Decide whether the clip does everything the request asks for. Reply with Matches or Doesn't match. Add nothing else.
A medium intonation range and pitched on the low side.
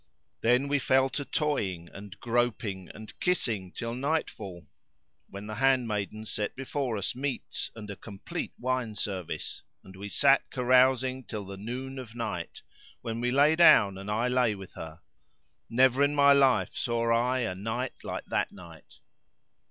Matches